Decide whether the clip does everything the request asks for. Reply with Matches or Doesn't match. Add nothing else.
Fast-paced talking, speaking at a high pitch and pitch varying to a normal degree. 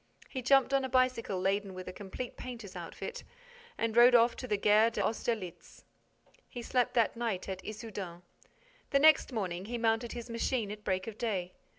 Doesn't match